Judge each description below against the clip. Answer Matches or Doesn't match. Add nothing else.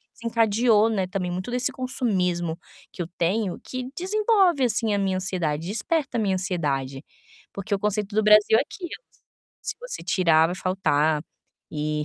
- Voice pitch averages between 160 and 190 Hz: Doesn't match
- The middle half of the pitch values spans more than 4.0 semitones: Matches